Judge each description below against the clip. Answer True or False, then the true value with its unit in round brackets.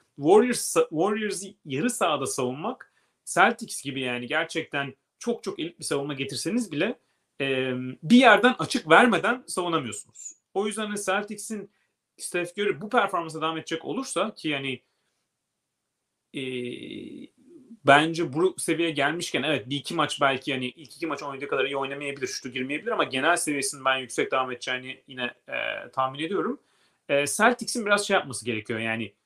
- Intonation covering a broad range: True (7.4 semitones)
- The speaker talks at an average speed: False (145 wpm)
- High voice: False (155 Hz)